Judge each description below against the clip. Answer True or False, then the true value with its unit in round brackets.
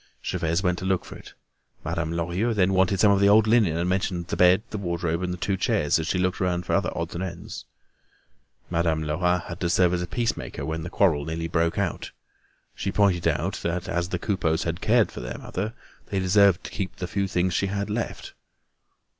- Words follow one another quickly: True (220 wpm)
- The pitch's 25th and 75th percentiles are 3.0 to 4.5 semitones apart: False (2.5 semitones)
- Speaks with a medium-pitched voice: False (90 Hz)